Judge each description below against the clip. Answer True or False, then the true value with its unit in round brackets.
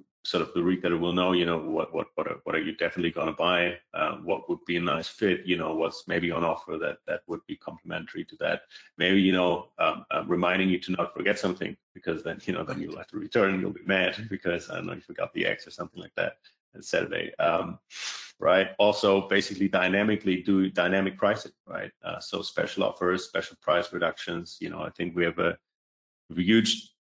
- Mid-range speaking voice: False (90 Hz)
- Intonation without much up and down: True (1.9 semitones)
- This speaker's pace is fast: True (220 wpm)